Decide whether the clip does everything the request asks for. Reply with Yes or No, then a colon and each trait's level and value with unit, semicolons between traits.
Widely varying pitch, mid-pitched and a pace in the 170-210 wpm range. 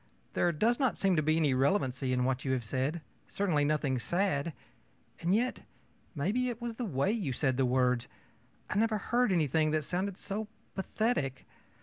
Yes: wide, 7.5 semitones; medium, 160 Hz; average, 180 wpm